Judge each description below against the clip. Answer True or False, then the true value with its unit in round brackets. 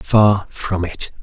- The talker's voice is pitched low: True (95 Hz)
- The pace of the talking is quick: False (145 wpm)